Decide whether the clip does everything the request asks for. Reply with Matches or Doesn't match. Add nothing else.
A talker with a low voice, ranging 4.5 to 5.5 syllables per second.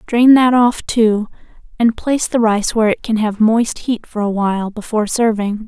Doesn't match